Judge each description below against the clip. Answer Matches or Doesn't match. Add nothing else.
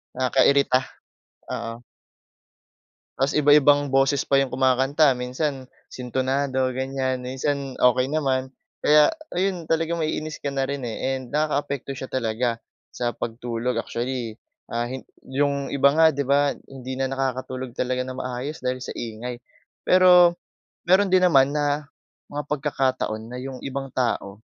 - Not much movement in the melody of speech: Matches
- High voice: Doesn't match